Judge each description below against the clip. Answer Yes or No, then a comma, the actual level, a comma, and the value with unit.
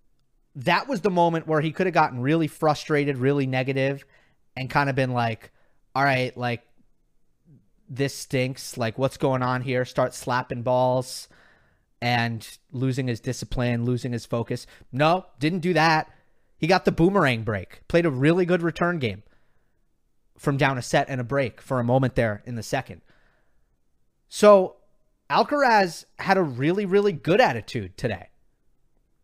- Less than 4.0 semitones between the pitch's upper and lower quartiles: No, average, 4.6 semitones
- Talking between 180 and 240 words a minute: No, average, 155 wpm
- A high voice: No, low, 130 Hz